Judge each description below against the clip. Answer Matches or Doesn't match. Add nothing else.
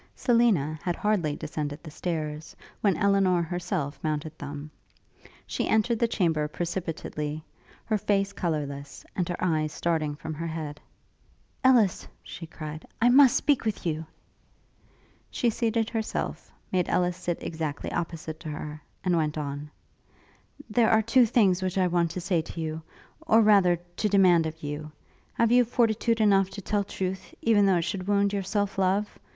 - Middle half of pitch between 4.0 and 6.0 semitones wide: Matches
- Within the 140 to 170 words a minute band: Matches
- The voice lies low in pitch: Doesn't match